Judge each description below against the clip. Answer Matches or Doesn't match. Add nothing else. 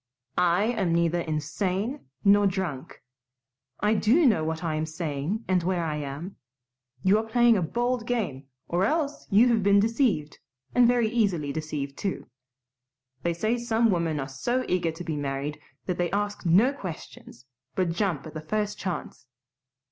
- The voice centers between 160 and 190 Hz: Matches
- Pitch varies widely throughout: Matches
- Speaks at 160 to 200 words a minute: Matches